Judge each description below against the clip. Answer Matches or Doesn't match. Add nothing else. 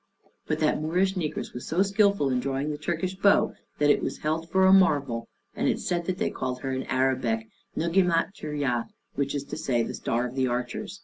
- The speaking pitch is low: Doesn't match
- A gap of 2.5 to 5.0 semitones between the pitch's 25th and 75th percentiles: Doesn't match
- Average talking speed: Doesn't match